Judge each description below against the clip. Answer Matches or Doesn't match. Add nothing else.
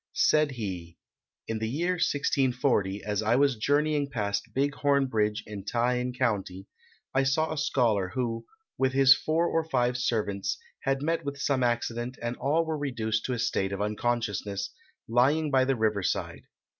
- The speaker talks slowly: Doesn't match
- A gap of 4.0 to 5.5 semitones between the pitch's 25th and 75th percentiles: Matches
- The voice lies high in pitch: Doesn't match